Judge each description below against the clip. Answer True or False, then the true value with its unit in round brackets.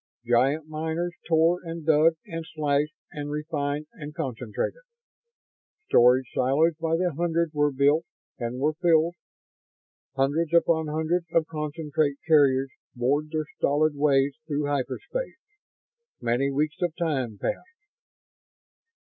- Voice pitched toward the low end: False (150 Hz)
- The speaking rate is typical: False (120 wpm)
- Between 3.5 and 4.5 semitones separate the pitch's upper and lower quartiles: False (2.6 semitones)